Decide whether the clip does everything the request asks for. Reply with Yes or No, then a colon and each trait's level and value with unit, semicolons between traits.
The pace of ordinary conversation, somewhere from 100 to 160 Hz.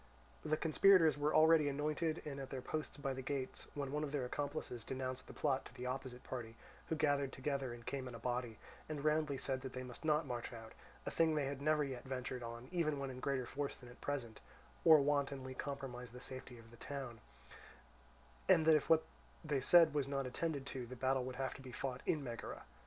No: fast, 220 wpm; low, 135 Hz